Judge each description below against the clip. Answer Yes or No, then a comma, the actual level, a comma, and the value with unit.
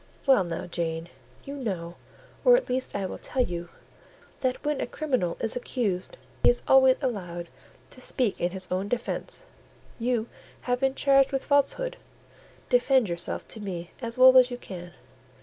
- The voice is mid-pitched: No, high, 245 Hz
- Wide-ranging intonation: Yes, wide, 6.7 semitones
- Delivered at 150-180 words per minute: Yes, average, 165 wpm